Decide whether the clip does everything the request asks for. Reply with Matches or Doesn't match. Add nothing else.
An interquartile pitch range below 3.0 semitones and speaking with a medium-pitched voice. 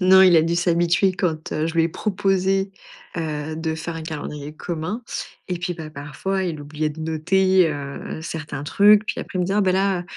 Doesn't match